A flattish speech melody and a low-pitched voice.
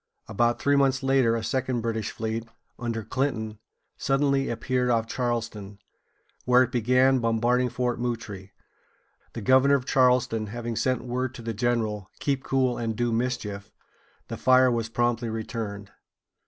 Yes: narrow, 2.2 semitones; low, 120 Hz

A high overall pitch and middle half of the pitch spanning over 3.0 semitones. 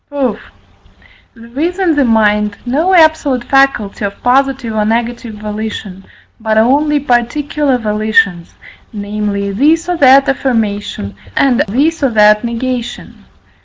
Yes: high, 235 Hz; average, 4.6 semitones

